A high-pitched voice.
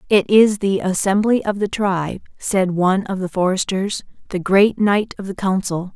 Yes: high, 195 Hz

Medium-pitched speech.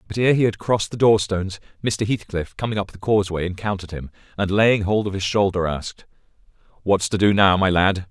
No: low, 100 Hz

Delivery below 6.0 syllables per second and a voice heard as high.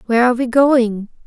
No: 6.3 syllables/s; high, 240 Hz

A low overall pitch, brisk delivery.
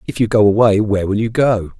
Yes: low, 105 Hz; fast, 265 wpm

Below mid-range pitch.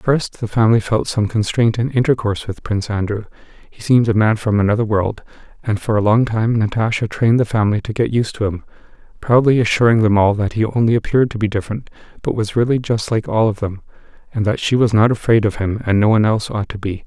Yes: low, 110 Hz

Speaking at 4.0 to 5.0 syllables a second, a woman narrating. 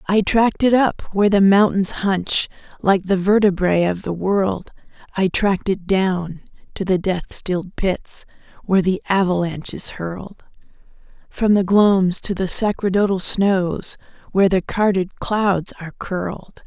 Yes: 4.3 syllables/s; female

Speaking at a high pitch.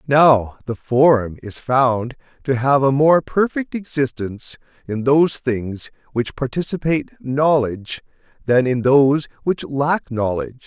No: low, 135 Hz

